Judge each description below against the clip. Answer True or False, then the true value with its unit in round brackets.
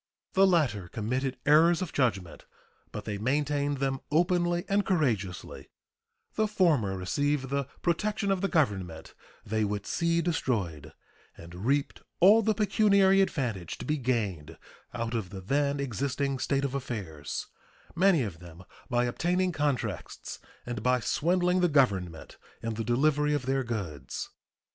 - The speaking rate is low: False (145 wpm)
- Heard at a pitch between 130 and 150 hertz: True (135 Hz)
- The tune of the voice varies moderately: False (8.1 semitones)